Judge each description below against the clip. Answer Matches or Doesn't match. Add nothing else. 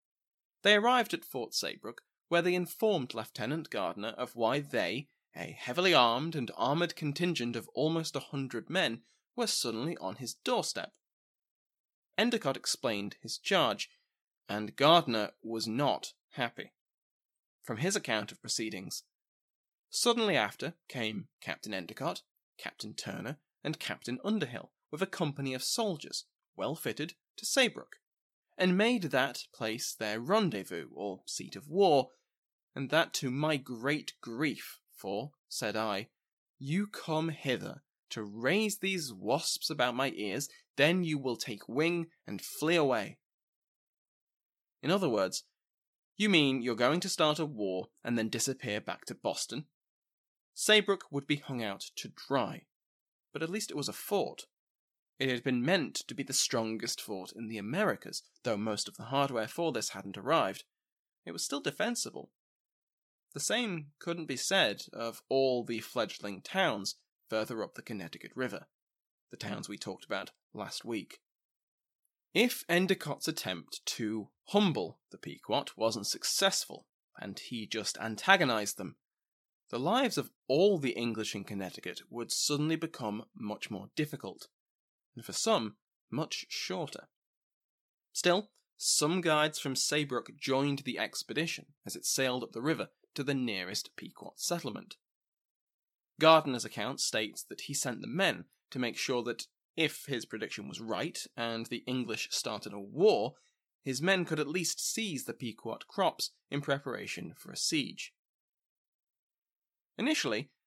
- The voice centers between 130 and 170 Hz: Matches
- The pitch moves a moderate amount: Doesn't match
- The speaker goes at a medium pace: Matches